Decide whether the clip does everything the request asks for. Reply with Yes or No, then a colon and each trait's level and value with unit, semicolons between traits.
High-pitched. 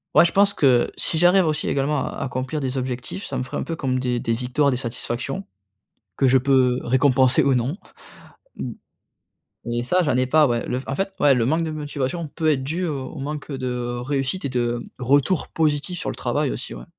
No: low, 135 Hz